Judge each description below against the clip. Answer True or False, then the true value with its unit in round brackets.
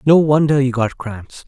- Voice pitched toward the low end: True (130 Hz)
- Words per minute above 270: False (205 wpm)